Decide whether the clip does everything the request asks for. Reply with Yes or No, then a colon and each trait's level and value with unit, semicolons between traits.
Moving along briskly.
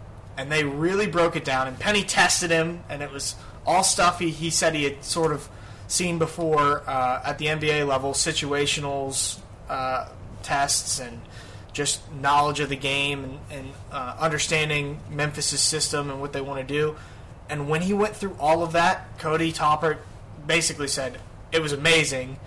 No: average, 170 wpm